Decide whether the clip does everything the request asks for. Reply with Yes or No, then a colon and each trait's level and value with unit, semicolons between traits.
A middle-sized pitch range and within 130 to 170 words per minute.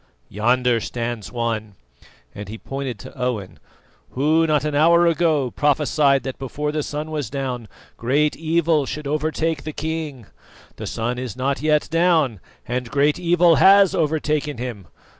Yes: average, 4.0 semitones; average, 150 wpm